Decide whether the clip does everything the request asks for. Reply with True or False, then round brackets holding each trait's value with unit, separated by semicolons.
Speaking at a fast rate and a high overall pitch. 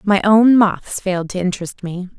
False (190 wpm; 195 Hz)